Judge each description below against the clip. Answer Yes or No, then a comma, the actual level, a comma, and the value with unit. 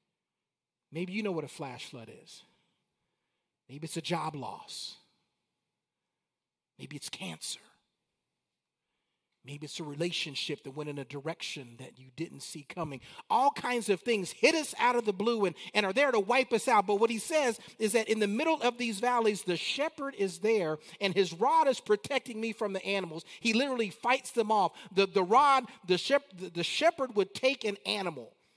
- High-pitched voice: Yes, high, 200 Hz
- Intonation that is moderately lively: No, wide, 6.5 semitones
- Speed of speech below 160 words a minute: No, average, 190 wpm